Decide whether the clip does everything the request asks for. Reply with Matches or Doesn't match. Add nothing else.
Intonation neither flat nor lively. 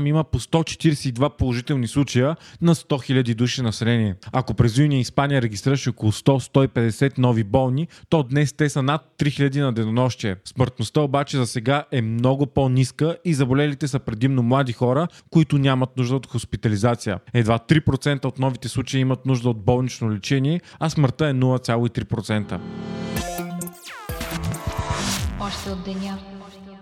Matches